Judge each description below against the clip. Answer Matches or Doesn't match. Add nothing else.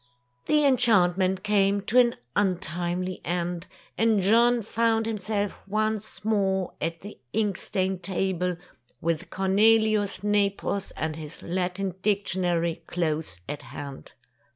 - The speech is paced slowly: Matches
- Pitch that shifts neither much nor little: Matches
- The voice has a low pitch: Doesn't match